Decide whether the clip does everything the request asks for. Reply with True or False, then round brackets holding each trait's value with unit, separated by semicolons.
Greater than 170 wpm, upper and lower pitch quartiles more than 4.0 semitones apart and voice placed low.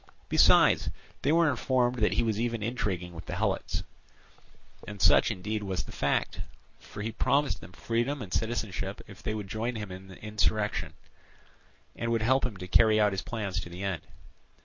False (180 wpm; 3.4 semitones; 110 Hz)